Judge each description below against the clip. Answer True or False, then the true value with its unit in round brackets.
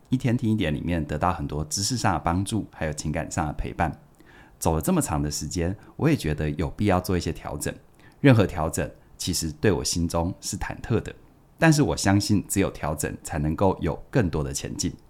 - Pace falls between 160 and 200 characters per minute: False (305 characters per minute)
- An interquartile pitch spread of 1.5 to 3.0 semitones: False (5.3 semitones)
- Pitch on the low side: True (85 Hz)